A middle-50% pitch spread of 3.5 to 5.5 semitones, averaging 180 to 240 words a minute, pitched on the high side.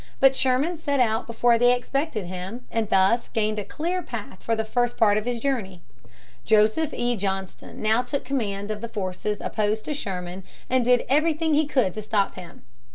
Yes: average, 4.0 semitones; average, 190 wpm; high, 230 Hz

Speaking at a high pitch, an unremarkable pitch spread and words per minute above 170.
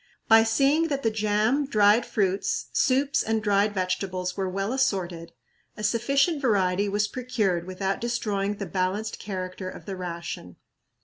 No: high, 205 Hz; average, 3.8 semitones; average, 145 wpm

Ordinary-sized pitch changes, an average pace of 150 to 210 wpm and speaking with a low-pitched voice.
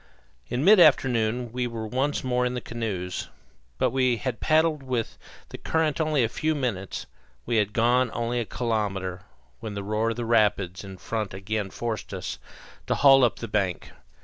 Yes: average, 3.4 semitones; average, 180 wpm; low, 115 Hz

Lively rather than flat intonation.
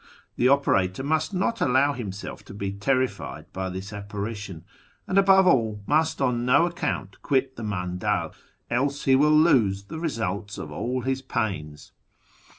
Yes: wide, 6.0 semitones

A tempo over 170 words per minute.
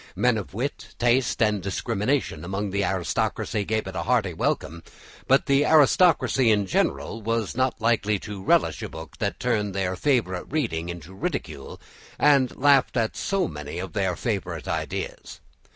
No: average, 160 wpm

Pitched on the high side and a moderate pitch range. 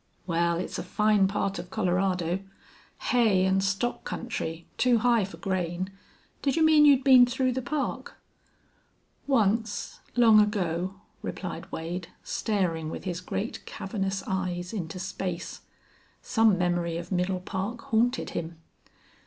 Yes: high, 195 Hz; average, 4.2 semitones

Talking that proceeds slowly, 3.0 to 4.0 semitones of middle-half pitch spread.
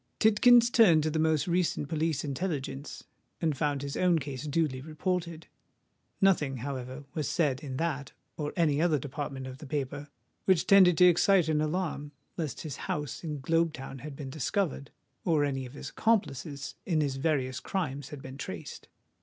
No: average, 170 wpm; average, 3.5 semitones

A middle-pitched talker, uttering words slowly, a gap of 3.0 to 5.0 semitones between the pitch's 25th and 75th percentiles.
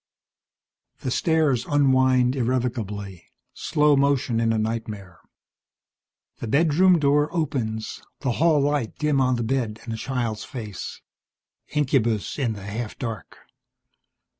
No: low, 125 Hz; slow, 120 wpm; average, 4.3 semitones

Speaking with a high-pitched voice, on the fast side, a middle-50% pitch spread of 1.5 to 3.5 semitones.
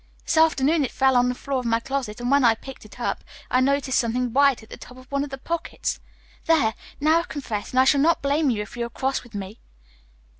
Yes: very high, 265 Hz; fast, 255 wpm; average, 2.8 semitones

